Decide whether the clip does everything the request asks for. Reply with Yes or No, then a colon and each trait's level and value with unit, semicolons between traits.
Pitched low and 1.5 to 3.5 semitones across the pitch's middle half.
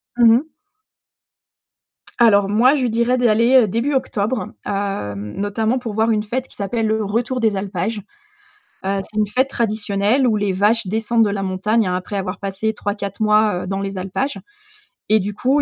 No: high, 215 Hz; average, 2.8 semitones